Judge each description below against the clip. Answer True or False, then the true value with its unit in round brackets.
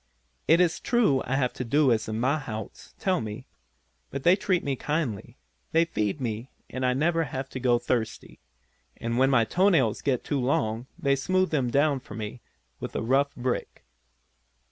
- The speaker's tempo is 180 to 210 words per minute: True (185 wpm)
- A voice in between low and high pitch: False (130 Hz)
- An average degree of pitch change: True (4.5 semitones)